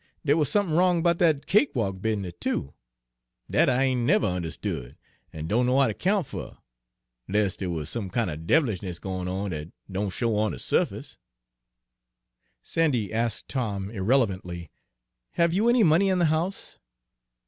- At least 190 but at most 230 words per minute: No, average, 160 wpm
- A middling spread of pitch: No, wide, 8.9 semitones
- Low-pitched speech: Yes, low, 115 Hz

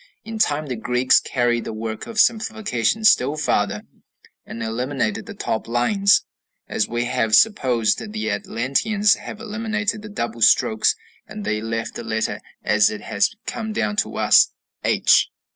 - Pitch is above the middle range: No, low, 125 Hz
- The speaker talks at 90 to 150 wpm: No, average, 160 wpm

